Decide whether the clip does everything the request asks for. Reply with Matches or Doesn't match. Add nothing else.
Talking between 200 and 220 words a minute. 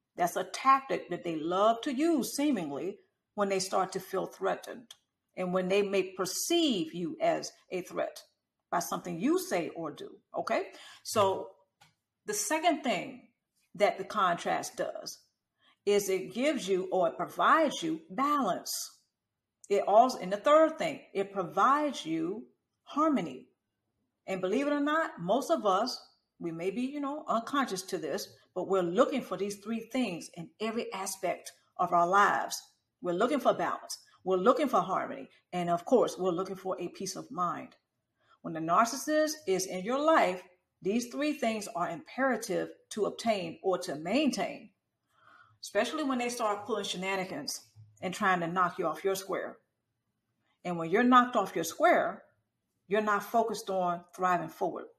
Doesn't match